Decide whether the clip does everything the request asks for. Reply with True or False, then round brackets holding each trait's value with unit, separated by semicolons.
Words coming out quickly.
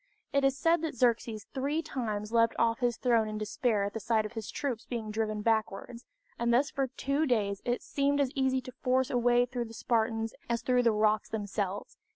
True (210 wpm)